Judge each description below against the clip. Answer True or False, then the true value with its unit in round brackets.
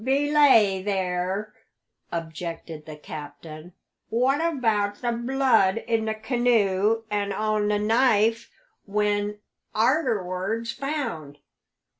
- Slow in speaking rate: True (95 wpm)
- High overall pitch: True (210 Hz)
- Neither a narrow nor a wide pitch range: True (3.9 semitones)